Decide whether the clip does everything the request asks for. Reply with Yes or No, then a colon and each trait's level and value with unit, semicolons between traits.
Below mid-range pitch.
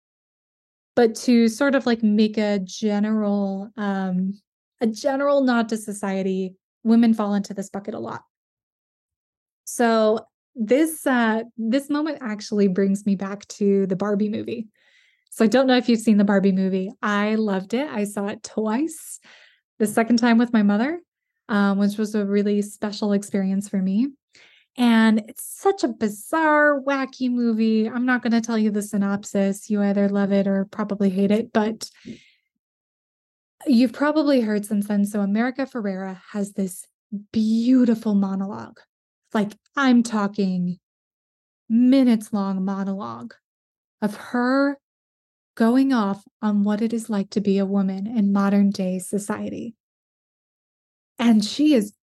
No: high, 215 Hz